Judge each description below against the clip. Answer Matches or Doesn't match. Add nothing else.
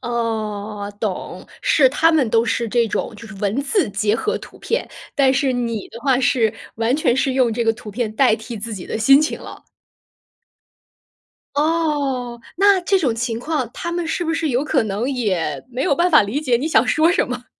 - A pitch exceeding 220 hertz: Matches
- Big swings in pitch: Doesn't match